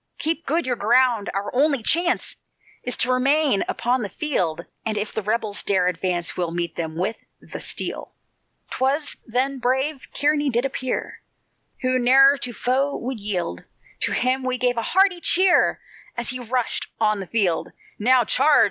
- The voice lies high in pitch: Yes, very high, 250 Hz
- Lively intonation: No, average, 4.7 semitones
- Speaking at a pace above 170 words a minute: No, average, 165 wpm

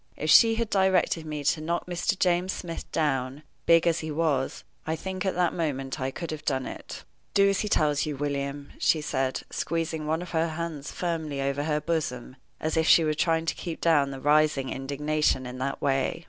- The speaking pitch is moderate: Yes, medium, 155 Hz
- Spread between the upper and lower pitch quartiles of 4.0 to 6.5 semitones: No, average, 3.2 semitones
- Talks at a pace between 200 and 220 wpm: Yes, fast, 205 wpm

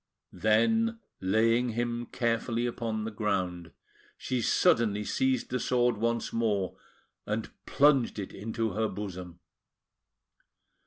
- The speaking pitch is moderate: No, low, 115 Hz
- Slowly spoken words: Yes, slow, 110 wpm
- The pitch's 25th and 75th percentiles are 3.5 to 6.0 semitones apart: No, narrow, 2.5 semitones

